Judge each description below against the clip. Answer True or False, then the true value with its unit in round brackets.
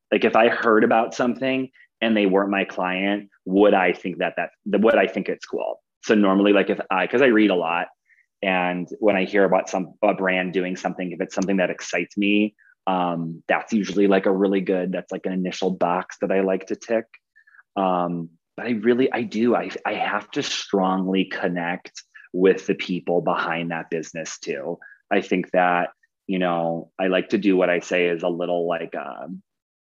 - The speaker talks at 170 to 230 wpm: True (200 wpm)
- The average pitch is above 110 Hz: False (95 Hz)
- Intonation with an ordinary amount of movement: False (2.1 semitones)